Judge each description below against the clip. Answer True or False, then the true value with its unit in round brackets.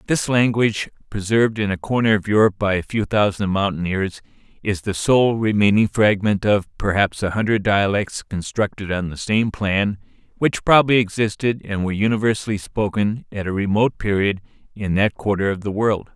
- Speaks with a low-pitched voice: True (105 Hz)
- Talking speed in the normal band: True (165 wpm)